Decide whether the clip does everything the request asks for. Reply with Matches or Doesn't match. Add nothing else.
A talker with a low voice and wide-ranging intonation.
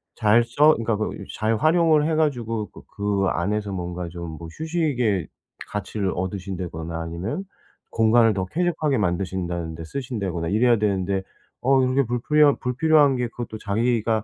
Matches